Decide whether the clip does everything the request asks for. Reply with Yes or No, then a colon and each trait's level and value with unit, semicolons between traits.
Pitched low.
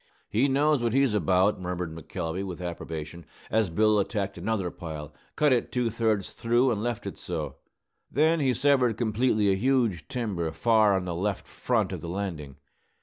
Yes: low, 105 Hz